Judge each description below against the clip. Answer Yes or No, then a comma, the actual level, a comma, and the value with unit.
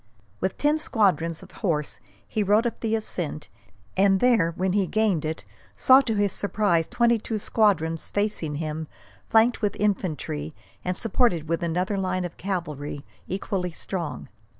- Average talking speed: Yes, average, 150 wpm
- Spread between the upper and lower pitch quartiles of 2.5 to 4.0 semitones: No, average, 4.6 semitones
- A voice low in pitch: No, high, 190 Hz